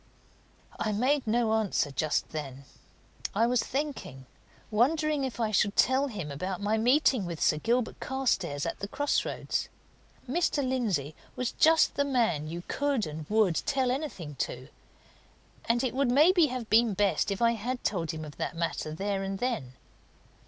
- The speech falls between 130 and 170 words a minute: Yes, average, 165 wpm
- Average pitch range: No, wide, 7.2 semitones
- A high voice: Yes, high, 220 Hz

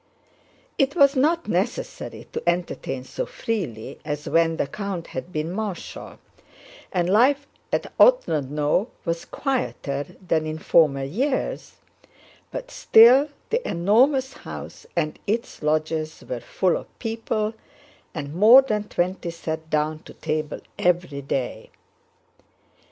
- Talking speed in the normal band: No, slow, 125 wpm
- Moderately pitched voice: Yes, medium, 175 Hz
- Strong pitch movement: Yes, wide, 7.2 semitones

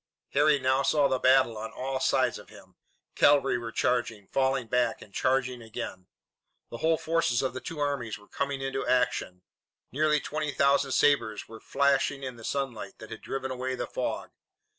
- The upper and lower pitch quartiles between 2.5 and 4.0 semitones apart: Yes, average, 2.8 semitones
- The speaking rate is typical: Yes, average, 180 wpm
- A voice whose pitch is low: Yes, low, 130 Hz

